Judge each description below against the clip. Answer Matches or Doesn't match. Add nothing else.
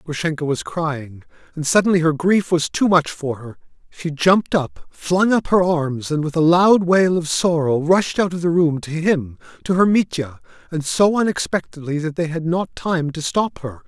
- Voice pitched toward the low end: Doesn't match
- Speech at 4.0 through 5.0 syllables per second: Matches